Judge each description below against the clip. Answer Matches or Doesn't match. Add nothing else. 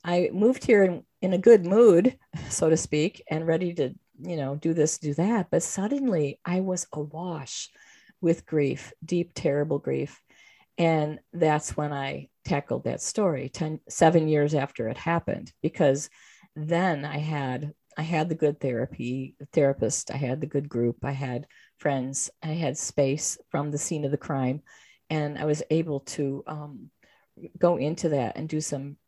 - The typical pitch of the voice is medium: Matches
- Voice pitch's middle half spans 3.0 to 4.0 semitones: Matches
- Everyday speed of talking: Matches